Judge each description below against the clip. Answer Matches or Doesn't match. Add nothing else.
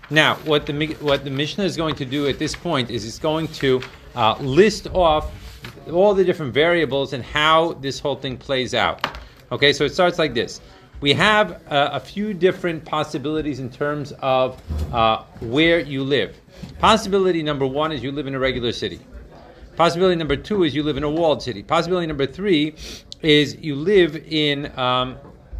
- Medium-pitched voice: Matches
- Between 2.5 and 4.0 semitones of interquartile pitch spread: Matches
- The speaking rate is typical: Doesn't match